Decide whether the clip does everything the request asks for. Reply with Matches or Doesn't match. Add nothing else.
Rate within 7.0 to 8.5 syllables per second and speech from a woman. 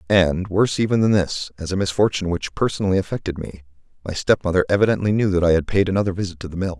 Doesn't match